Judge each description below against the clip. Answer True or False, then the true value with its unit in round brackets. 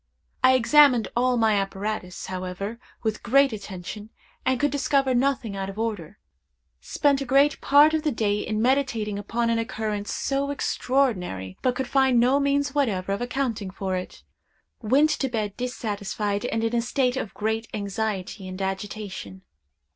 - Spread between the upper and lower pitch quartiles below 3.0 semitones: False (4.7 semitones)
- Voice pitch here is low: False (225 Hz)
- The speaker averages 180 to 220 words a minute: False (160 wpm)